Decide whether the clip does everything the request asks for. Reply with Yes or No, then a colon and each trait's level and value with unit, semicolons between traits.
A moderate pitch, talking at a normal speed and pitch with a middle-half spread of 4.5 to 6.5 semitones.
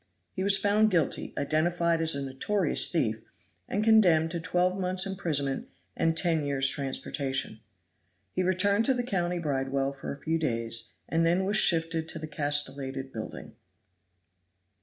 Yes: medium, 165 Hz; average, 150 wpm; average, 4.9 semitones